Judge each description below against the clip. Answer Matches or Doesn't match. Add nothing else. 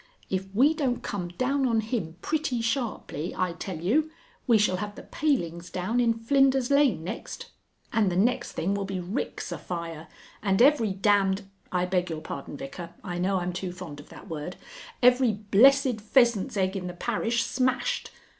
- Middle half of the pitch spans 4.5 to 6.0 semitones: Matches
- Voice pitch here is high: Matches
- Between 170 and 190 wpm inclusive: Matches